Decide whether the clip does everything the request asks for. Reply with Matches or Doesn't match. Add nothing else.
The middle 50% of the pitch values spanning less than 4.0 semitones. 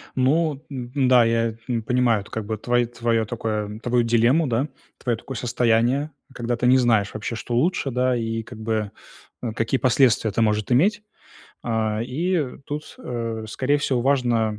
Matches